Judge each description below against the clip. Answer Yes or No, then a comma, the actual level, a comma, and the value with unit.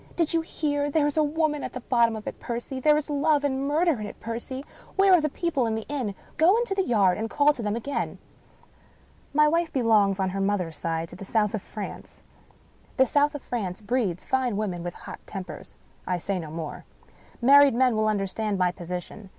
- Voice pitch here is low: No, high, 235 Hz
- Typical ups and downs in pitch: No, wide, 6.5 semitones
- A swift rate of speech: Yes, fast, 215 wpm